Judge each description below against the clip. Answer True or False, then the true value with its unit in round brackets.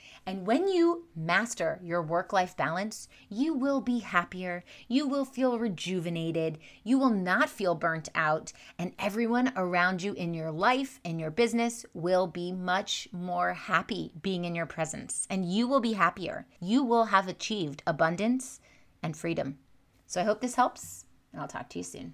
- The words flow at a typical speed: True (170 wpm)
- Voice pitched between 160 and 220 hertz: True (185 Hz)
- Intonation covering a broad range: True (5.8 semitones)